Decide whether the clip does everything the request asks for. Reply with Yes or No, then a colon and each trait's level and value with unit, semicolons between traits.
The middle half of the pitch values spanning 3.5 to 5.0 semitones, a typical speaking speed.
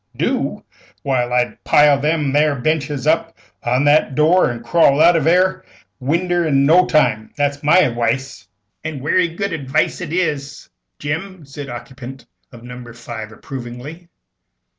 Yes: average, 4.5 semitones; average, 160 wpm